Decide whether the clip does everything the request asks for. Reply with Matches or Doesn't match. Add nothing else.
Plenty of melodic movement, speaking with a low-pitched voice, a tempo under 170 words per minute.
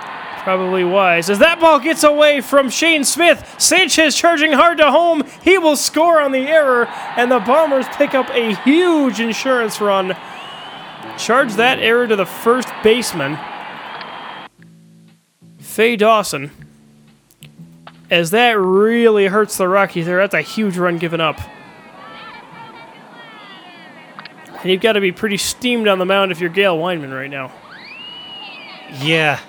Doesn't match